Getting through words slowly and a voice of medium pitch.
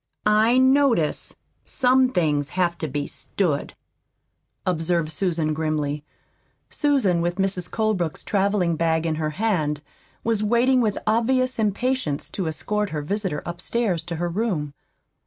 Yes: slow, 130 wpm; medium, 180 Hz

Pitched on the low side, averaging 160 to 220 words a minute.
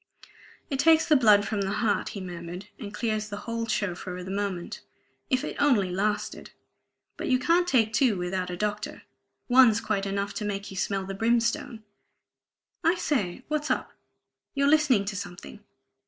No: high, 210 Hz; average, 170 wpm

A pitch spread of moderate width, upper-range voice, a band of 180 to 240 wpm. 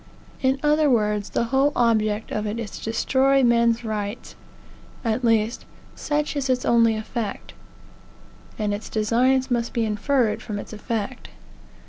No: average, 3.3 semitones; high, 230 Hz; average, 145 wpm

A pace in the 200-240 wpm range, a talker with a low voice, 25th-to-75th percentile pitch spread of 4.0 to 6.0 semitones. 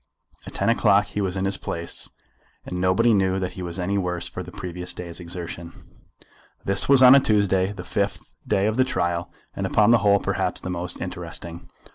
No: fast, 205 wpm; very low, 95 Hz; narrow, 2.4 semitones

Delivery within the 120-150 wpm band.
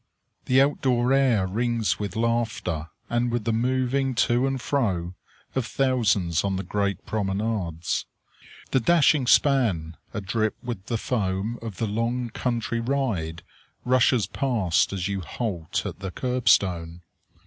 Yes: average, 140 wpm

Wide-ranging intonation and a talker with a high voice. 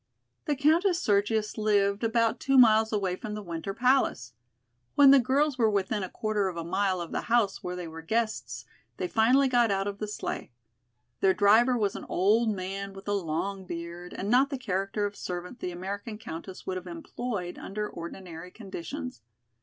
No: average, 3.9 semitones; high, 200 Hz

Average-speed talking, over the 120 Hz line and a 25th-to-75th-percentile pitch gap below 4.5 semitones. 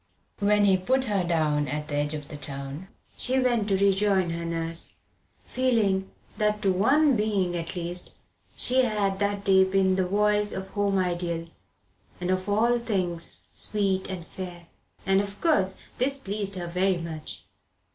Yes: average, 170 wpm; high, 190 Hz; average, 3.2 semitones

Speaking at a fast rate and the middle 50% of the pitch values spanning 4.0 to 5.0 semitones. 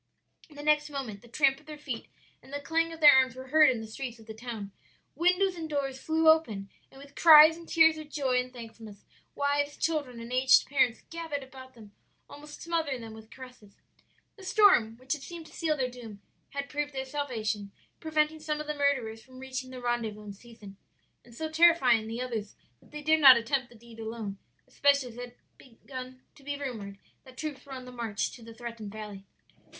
Yes: fast, 210 wpm; average, 4.5 semitones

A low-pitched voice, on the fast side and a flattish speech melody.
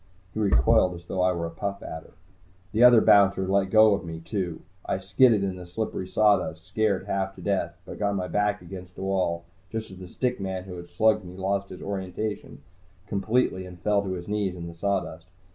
Yes: very low, 95 Hz; fast, 210 wpm; narrow, 2.3 semitones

